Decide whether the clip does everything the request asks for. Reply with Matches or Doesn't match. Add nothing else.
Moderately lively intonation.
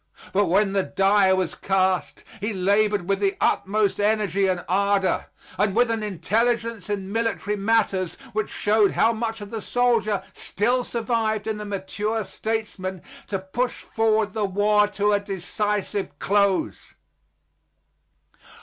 Doesn't match